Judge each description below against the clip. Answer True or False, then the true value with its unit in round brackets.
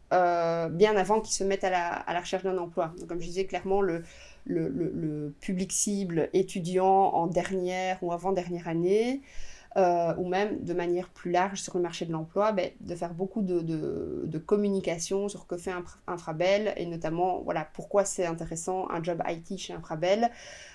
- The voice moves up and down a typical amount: False (2.1 semitones)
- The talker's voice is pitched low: False (180 Hz)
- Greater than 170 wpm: True (190 wpm)